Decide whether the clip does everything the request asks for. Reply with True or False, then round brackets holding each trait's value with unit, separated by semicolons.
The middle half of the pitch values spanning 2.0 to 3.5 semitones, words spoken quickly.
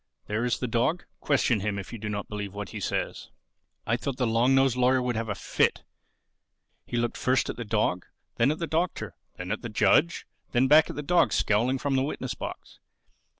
False (3.9 semitones; 215 wpm)